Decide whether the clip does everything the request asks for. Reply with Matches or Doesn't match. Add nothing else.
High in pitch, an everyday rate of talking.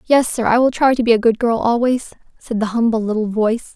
Doesn't match